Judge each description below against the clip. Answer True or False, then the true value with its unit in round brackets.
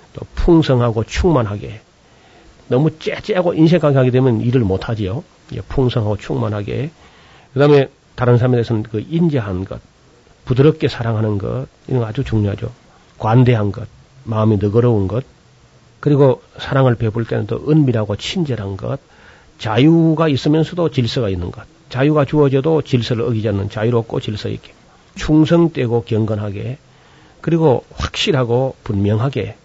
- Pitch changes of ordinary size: True (4.8 semitones)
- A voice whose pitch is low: True (125 Hz)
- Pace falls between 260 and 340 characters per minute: True (320 characters per minute)